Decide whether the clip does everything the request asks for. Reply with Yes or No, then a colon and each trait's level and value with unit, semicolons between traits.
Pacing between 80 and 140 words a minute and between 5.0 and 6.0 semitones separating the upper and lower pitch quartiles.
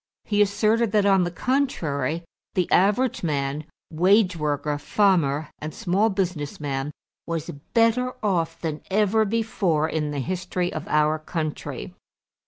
Yes: slow, 135 wpm; average, 5.3 semitones